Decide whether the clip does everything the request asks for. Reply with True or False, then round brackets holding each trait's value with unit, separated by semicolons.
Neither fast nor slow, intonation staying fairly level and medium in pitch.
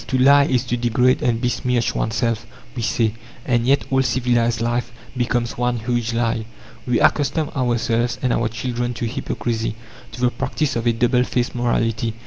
False (170 wpm; 1.4 semitones; 120 Hz)